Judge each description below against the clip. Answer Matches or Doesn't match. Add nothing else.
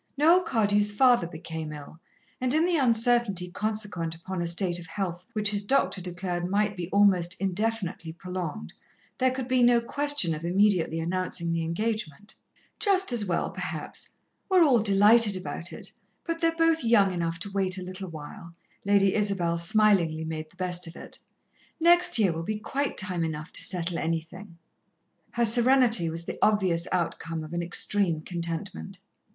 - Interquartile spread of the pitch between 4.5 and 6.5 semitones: Matches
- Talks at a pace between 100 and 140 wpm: Doesn't match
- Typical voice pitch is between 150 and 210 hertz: Matches